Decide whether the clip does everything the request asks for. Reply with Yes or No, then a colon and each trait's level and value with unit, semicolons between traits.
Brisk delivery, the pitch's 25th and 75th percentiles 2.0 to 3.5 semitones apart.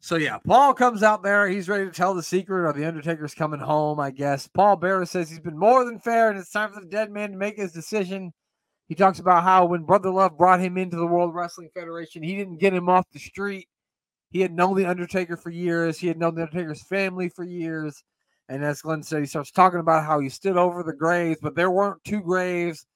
Yes: fast, 245 wpm; average, 2.8 semitones